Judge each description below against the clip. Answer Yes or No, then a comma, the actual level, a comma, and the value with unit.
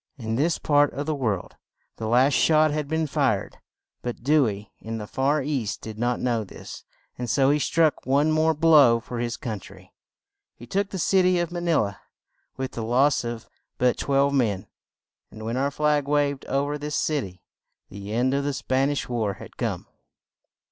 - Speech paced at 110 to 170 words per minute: No, average, 200 wpm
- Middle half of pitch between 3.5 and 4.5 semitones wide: Yes, average, 4.2 semitones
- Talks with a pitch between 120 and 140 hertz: Yes, low, 135 Hz